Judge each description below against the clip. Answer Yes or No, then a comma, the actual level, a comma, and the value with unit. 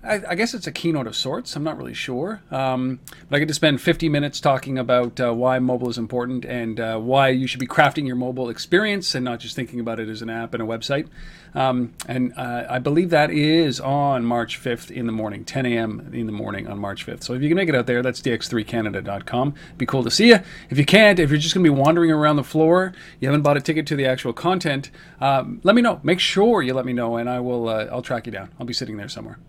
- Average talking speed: No, fast, 265 wpm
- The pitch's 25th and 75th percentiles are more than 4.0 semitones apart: Yes, average, 4.8 semitones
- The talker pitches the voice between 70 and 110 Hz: No, low, 130 Hz